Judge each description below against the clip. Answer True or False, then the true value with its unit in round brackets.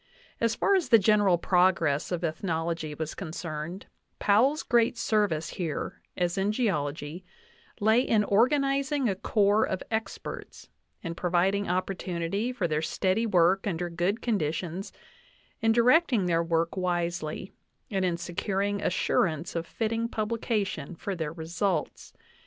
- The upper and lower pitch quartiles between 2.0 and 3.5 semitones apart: False (4.5 semitones)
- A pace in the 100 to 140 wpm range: True (135 wpm)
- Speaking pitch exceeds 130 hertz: True (185 Hz)